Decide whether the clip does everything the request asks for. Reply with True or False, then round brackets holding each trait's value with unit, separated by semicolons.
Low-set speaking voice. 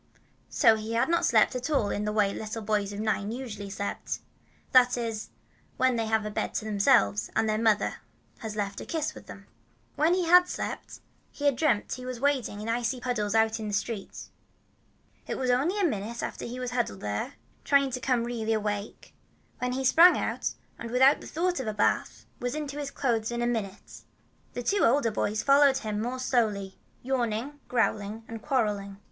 False (230 Hz)